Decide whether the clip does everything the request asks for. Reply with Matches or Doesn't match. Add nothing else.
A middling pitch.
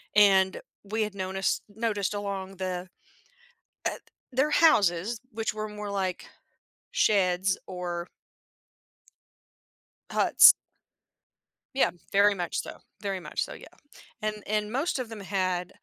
Doesn't match